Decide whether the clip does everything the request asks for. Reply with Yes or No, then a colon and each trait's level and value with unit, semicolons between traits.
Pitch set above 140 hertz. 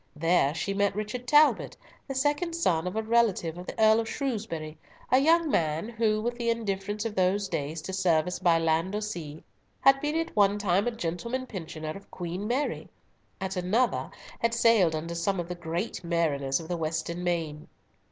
Yes: high, 190 Hz